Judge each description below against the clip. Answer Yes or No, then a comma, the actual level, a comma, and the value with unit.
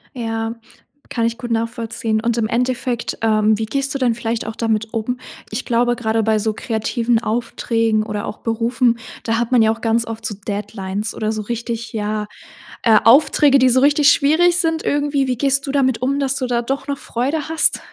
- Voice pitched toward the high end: Yes, high, 235 Hz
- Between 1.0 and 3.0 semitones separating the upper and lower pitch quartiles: Yes, average, 2.7 semitones